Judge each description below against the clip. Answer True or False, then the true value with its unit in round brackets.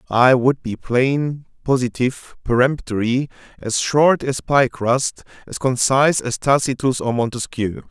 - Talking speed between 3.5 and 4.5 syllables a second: True (4.2 syllables/s)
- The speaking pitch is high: False (130 Hz)